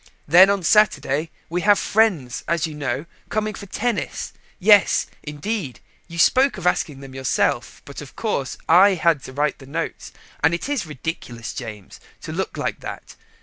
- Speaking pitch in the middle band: Yes, medium, 165 Hz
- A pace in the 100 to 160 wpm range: No, average, 170 wpm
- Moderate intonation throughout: No, wide, 6.3 semitones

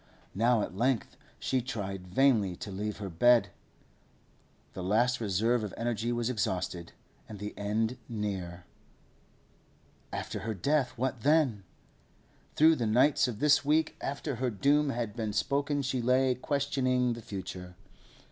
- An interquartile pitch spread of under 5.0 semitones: Yes, average, 4.3 semitones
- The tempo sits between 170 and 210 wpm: No, average, 140 wpm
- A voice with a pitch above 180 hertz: No, low, 120 Hz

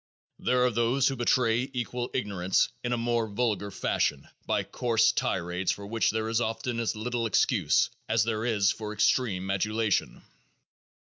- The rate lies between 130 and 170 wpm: Yes, average, 165 wpm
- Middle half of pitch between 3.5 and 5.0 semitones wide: No, narrow, 2.4 semitones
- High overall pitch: No, low, 115 Hz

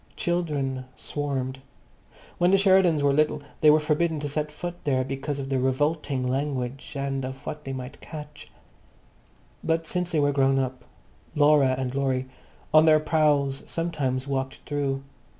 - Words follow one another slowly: No, average, 155 wpm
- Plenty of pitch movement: No, narrow, 2.5 semitones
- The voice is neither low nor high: Yes, medium, 145 Hz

